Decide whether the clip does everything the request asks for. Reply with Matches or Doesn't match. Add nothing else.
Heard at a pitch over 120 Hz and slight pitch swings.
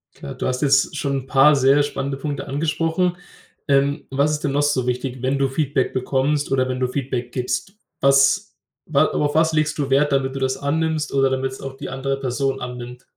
Matches